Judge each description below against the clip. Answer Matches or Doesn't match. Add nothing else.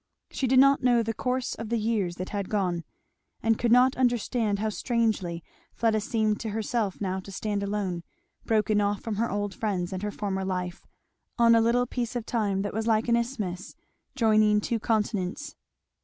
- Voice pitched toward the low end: Doesn't match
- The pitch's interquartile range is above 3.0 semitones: Doesn't match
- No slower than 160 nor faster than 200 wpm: Matches